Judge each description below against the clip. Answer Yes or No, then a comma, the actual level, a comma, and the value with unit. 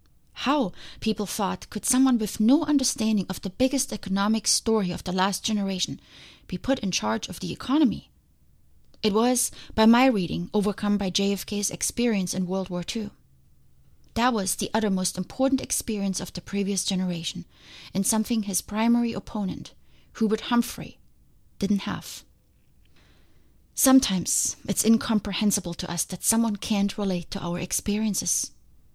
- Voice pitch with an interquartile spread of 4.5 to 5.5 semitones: No, average, 3.3 semitones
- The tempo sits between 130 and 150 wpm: Yes, average, 140 wpm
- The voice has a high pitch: Yes, high, 200 Hz